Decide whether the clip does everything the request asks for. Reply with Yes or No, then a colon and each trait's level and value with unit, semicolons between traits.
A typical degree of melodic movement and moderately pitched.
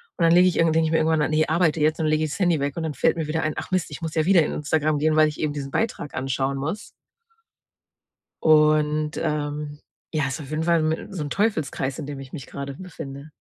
No: narrow, 1.8 semitones; medium, 155 Hz